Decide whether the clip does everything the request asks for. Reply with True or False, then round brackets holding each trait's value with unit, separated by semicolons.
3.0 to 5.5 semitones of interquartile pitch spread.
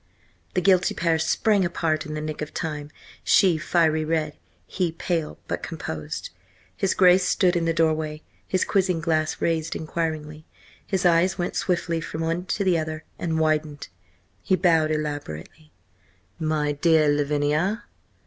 False (2.4 semitones)